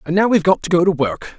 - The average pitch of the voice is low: No, medium, 175 Hz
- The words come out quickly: Yes, fast, 345 wpm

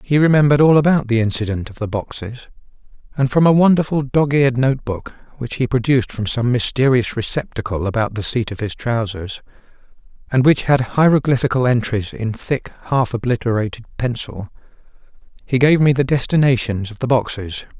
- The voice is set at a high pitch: No, low, 125 Hz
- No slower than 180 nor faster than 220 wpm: No, average, 160 wpm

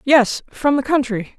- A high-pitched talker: Yes, very high, 260 Hz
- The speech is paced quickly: No, slow, 130 wpm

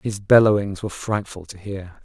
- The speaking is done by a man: Yes, male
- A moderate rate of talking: Yes, average, 175 wpm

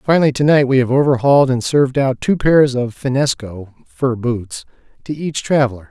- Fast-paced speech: No, average, 185 wpm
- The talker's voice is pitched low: Yes, low, 130 Hz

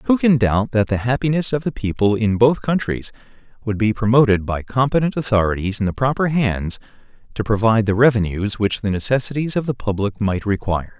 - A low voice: Yes, low, 115 Hz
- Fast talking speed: No, average, 185 wpm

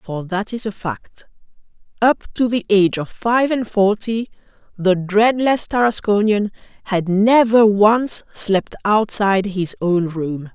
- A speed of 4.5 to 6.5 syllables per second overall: No, 3.9 syllables/s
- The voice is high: Yes, high, 205 Hz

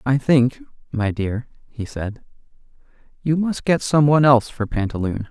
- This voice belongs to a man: Yes, male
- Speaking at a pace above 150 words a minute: No, average, 145 wpm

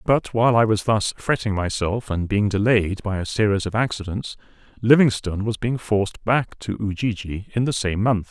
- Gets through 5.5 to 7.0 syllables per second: No, 5.1 syllables/s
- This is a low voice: Yes, low, 105 Hz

